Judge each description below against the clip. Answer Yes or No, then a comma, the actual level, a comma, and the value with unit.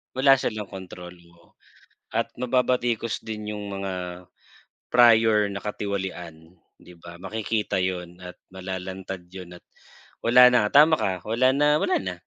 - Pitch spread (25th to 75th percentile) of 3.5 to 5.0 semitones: Yes, average, 4.5 semitones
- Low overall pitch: Yes, low, 100 Hz